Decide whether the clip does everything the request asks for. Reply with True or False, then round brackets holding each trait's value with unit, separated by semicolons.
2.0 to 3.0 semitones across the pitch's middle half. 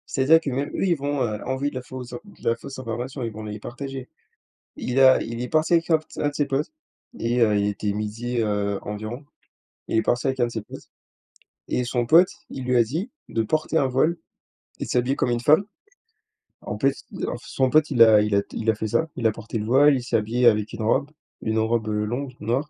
False (3.8 semitones)